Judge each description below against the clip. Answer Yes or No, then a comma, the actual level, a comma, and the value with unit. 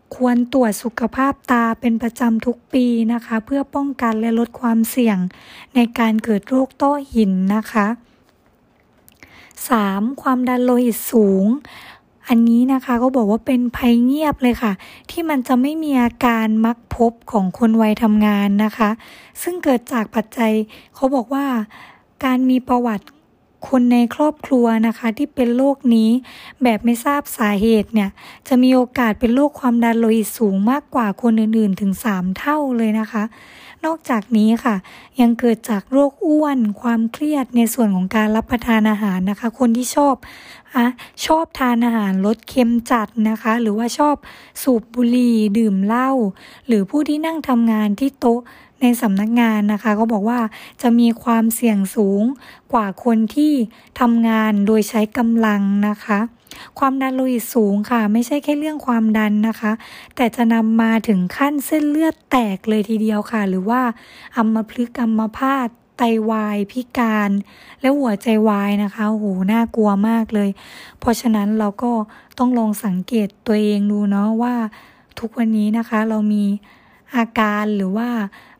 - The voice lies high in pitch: Yes, high, 230 Hz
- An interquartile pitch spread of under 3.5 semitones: Yes, average, 2.7 semitones